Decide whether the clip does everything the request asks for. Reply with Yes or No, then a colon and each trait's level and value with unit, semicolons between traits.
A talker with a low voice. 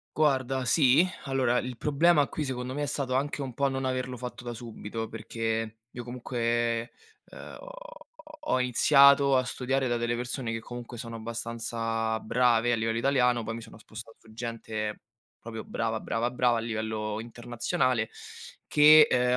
Yes: low, 120 Hz